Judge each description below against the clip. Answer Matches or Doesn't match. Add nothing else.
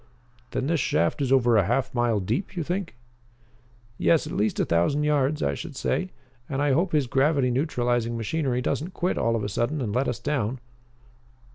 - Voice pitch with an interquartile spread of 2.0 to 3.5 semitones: Doesn't match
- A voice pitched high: Doesn't match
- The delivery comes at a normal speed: Matches